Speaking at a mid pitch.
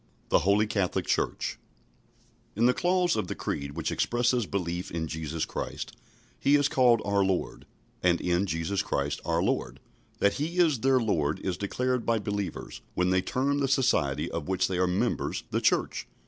No: low, 100 Hz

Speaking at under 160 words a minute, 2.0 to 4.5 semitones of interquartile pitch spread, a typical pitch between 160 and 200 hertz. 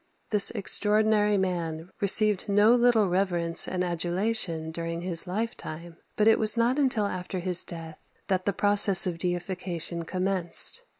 Yes: average, 140 wpm; average, 3.5 semitones; medium, 185 Hz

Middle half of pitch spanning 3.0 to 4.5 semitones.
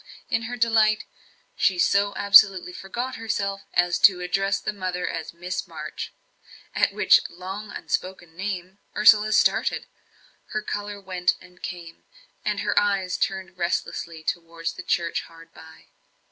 No: narrow, 2.6 semitones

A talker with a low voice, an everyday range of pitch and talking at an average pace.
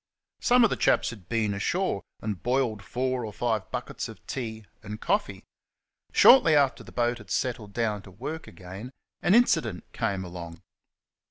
Yes: low, 115 Hz; average, 4.7 semitones; average, 165 wpm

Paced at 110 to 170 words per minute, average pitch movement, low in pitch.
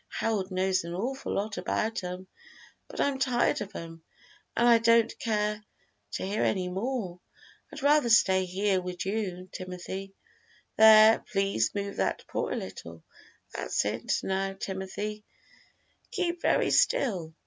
No: average, 140 wpm; average, 3.4 semitones; high, 195 Hz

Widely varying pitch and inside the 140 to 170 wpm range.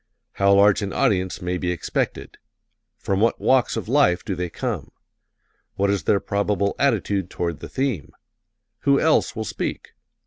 No: average, 3.6 semitones; average, 160 wpm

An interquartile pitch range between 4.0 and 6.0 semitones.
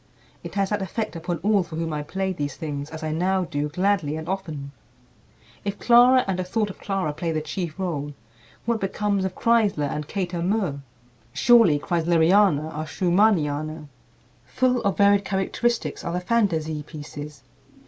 Yes: average, 4.5 semitones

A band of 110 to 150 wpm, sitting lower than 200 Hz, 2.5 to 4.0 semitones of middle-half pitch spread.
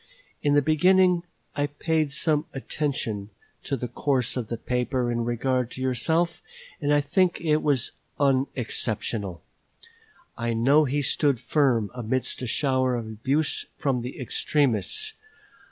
Yes: slow, 135 wpm; low, 135 Hz; average, 3.6 semitones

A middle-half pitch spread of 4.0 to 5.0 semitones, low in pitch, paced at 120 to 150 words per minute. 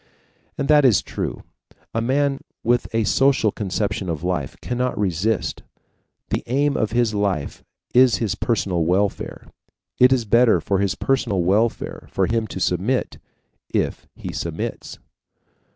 Yes: average, 4.4 semitones; low, 110 Hz; average, 140 wpm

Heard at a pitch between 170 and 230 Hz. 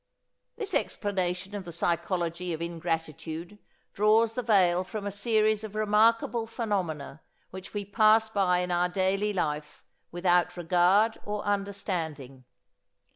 Yes: high, 190 Hz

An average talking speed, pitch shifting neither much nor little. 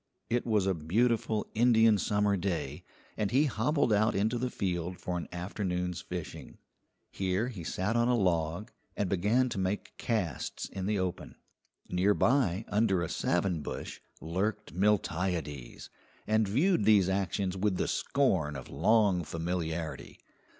Yes: average, 145 wpm; average, 3.7 semitones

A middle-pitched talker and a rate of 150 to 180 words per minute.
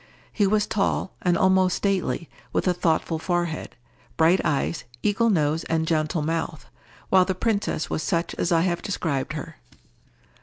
Yes: medium, 175 Hz; average, 155 wpm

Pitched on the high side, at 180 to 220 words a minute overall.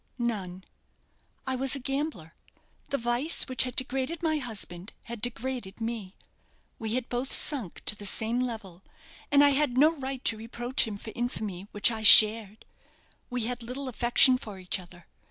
No: high, 240 Hz; average, 170 wpm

